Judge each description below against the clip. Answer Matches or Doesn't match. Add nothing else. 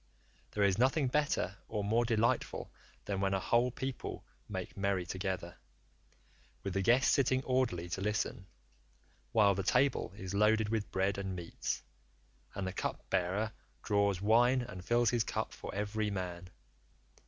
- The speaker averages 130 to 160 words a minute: Matches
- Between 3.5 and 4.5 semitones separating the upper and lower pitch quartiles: Matches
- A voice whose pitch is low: Matches